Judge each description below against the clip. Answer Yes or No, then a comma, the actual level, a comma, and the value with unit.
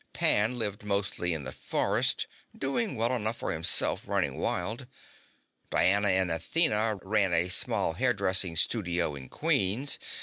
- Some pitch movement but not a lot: Yes, average, 4.4 semitones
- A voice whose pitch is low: Yes, low, 100 Hz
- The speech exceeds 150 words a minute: No, slow, 135 wpm